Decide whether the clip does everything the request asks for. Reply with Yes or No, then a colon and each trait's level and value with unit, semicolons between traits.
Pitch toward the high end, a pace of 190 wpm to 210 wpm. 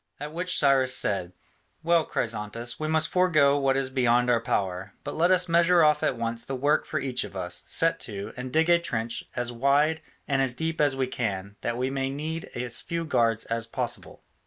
No: low, 135 Hz; fast, 205 wpm